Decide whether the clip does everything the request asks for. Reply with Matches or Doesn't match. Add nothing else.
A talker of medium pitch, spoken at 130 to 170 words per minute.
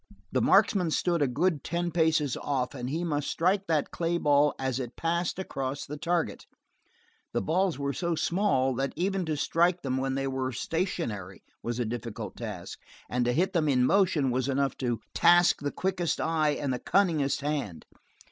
Doesn't match